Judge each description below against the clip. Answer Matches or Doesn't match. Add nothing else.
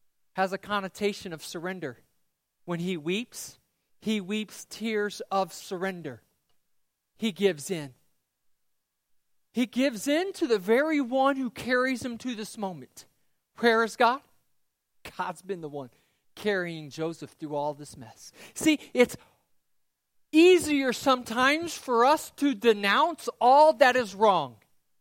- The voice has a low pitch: Doesn't match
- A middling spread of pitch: Doesn't match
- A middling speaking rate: Doesn't match